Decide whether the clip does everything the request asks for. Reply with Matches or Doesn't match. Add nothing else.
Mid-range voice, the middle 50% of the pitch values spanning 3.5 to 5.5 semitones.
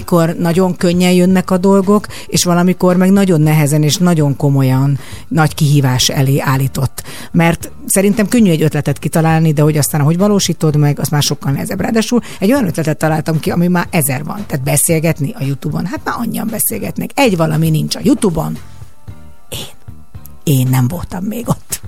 Matches